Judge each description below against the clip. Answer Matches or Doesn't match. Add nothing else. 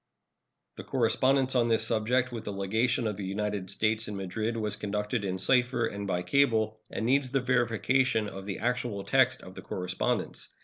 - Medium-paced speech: Matches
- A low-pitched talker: Matches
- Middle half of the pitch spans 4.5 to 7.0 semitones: Doesn't match